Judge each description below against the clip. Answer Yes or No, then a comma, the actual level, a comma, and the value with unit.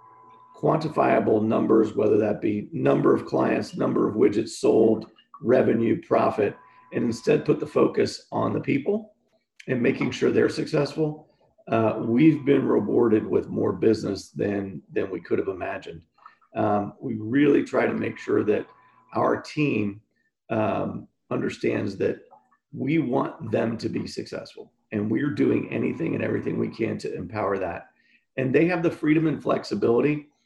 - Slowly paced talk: No, average, 150 wpm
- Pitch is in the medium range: Yes, medium, 155 Hz